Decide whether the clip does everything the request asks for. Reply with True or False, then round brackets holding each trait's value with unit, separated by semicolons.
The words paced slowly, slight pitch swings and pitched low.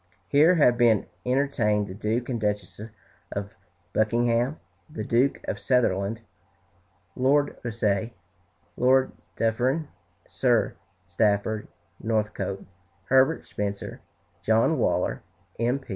False (100 wpm; 3.7 semitones; 115 Hz)